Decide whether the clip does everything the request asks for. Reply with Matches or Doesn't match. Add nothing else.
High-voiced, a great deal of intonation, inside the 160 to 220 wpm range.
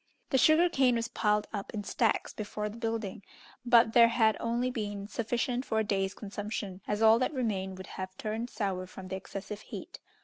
Doesn't match